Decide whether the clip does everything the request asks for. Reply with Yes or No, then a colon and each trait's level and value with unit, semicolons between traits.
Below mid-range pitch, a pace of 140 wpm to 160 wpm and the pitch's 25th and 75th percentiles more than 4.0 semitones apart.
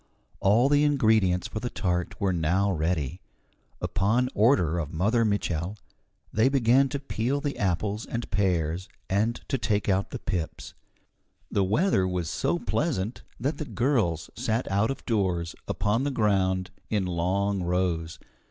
Yes: low, 100 Hz; average, 150 wpm; average, 4.6 semitones